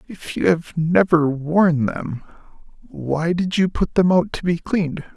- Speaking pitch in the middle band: Yes, medium, 165 Hz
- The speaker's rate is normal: Yes, average, 175 wpm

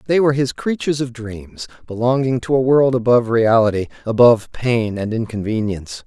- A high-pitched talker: No, low, 120 Hz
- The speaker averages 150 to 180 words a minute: Yes, average, 160 wpm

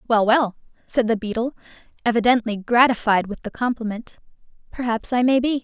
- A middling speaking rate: Yes, average, 150 wpm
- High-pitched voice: Yes, high, 235 Hz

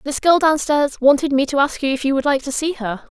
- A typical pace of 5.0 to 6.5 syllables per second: Yes, 5.7 syllables/s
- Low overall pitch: No, very high, 280 Hz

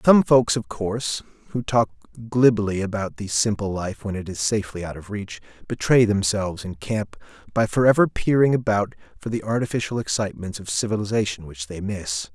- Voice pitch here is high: No, low, 105 Hz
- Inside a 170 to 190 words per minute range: Yes, average, 175 wpm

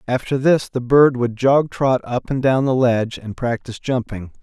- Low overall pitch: Yes, low, 125 Hz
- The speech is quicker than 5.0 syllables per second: No, 4.9 syllables/s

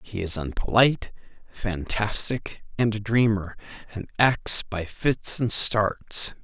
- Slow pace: Yes, slow, 120 wpm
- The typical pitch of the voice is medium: No, low, 105 Hz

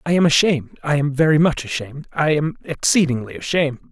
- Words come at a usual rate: Yes, average, 155 wpm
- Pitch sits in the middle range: Yes, medium, 150 Hz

